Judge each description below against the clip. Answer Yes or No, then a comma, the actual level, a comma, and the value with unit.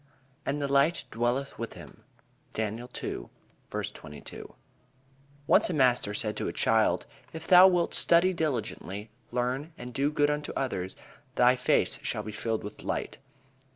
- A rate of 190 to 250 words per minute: No, average, 150 wpm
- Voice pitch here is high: No, low, 125 Hz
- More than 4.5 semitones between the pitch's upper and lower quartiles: Yes, average, 5.0 semitones